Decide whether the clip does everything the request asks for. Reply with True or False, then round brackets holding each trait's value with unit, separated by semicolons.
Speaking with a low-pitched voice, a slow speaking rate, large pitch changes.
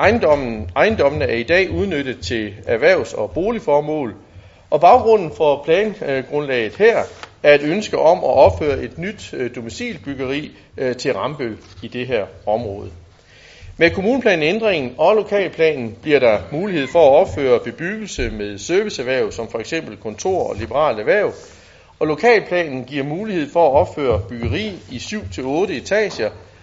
False (145 Hz; 135 wpm; 8.4 semitones)